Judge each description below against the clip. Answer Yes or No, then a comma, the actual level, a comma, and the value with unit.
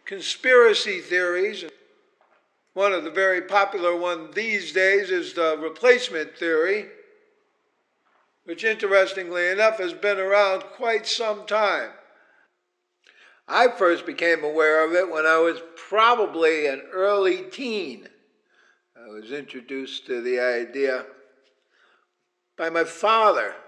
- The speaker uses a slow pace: Yes, slow, 115 wpm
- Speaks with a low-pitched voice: No, high, 190 Hz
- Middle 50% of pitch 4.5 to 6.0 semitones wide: Yes, average, 5.3 semitones